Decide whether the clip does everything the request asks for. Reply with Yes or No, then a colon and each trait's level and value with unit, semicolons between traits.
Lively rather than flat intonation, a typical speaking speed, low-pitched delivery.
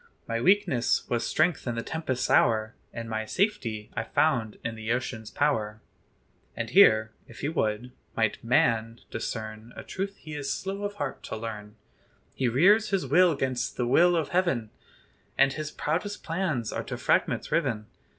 Yes: wide, 6.7 semitones; average, 170 wpm; low, 125 Hz